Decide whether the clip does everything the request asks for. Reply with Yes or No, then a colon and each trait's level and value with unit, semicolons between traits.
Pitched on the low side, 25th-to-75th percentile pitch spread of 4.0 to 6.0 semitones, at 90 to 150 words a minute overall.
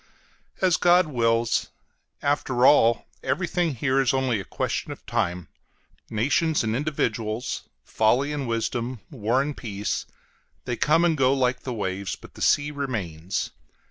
Yes: low, 125 Hz; average, 4.5 semitones; average, 140 wpm